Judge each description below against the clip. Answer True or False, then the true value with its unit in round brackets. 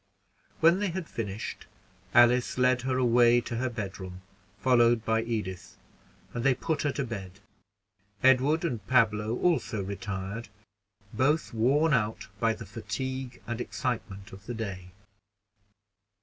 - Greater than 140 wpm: False (135 wpm)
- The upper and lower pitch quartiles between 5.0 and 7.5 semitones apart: False (3.6 semitones)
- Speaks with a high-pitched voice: False (120 Hz)